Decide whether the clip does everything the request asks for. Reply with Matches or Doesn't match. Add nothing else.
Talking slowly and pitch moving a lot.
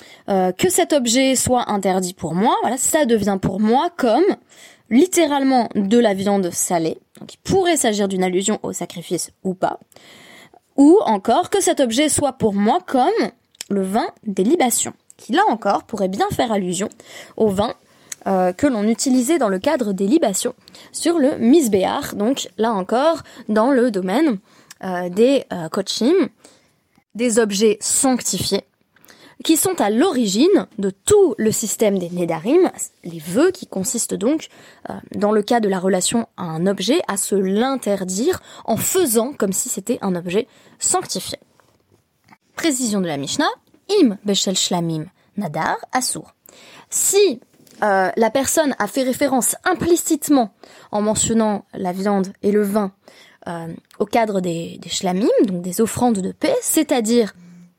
Doesn't match